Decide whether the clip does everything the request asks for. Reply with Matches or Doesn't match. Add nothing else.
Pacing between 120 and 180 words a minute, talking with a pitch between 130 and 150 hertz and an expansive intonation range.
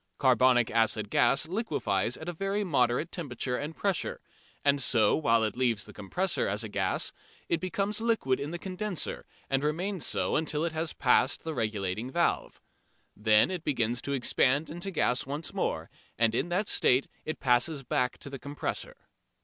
Matches